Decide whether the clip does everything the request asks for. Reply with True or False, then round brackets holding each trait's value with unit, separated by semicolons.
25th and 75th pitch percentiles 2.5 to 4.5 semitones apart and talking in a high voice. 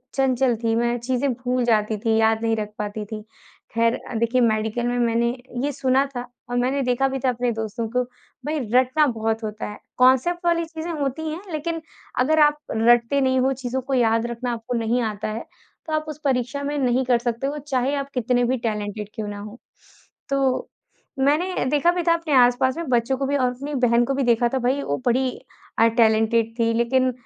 True (3.0 semitones; 250 Hz)